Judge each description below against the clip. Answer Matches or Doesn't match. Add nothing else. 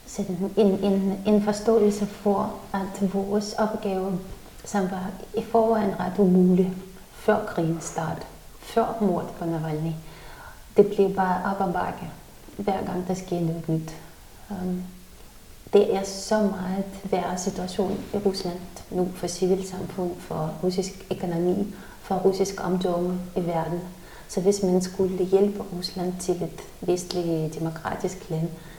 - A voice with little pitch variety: Matches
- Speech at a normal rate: Doesn't match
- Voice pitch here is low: Doesn't match